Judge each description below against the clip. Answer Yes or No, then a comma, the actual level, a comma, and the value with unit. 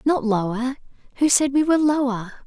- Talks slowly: No, average, 170 wpm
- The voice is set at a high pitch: Yes, very high, 260 Hz